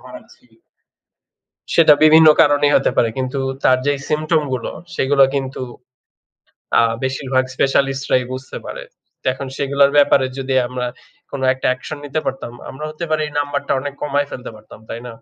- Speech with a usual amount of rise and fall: No, narrow, 1.8 semitones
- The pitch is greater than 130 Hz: Yes, medium, 140 Hz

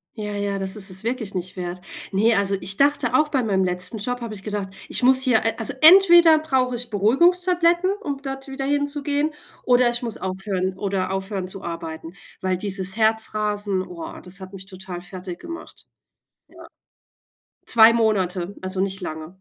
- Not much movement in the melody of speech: No, wide, 5.5 semitones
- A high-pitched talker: Yes, high, 205 Hz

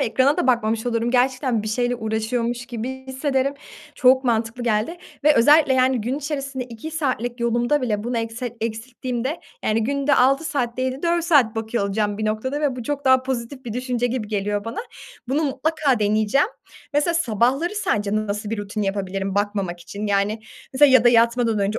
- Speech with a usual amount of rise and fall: Yes, average, 3.4 semitones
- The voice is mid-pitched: No, high, 240 Hz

